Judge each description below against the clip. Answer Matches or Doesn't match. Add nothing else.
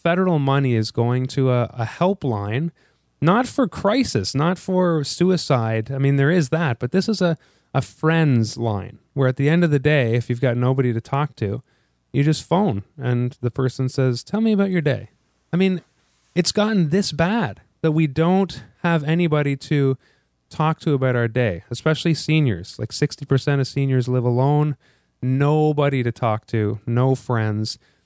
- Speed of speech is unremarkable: Matches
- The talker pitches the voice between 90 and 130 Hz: Doesn't match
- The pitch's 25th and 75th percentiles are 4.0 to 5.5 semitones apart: Matches